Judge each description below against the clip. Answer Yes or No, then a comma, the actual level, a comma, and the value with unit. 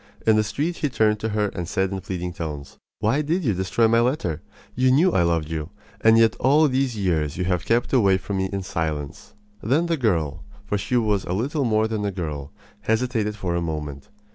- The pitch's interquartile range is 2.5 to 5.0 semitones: No, wide, 5.6 semitones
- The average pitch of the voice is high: No, low, 105 Hz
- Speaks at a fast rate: Yes, fast, 215 wpm